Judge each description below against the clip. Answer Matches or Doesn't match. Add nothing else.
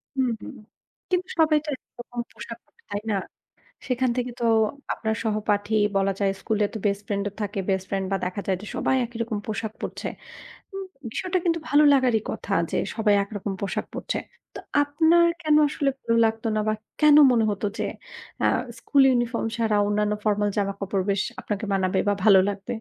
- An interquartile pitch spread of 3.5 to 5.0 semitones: Matches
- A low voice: Doesn't match